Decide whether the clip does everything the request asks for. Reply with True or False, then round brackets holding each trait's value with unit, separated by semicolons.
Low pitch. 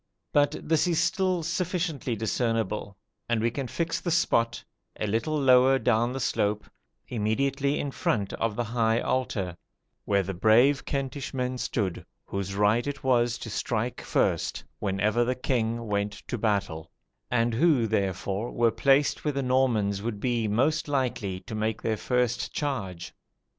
True (120 Hz)